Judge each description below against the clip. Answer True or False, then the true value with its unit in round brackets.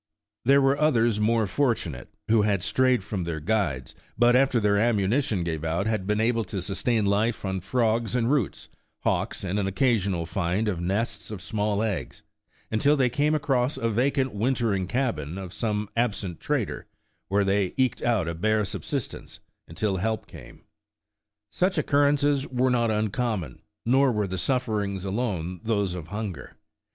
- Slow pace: False (165 wpm)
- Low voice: True (110 Hz)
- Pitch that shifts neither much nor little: True (4.1 semitones)